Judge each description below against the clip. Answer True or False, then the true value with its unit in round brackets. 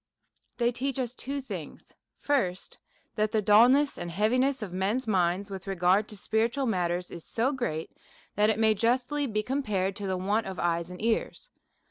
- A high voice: True (215 Hz)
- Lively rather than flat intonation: False (4.9 semitones)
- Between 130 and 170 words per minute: False (180 wpm)